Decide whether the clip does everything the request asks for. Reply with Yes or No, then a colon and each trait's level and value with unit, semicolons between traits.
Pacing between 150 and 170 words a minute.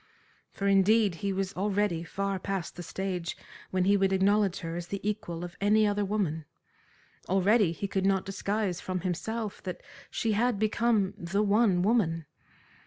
Yes: average, 165 wpm